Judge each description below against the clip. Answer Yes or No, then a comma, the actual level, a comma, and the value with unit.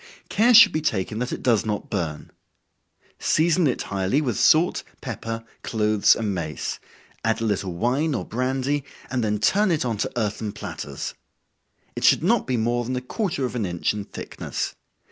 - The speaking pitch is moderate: No, low, 120 Hz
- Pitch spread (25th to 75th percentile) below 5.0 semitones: No, wide, 5.5 semitones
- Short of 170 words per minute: No, average, 180 wpm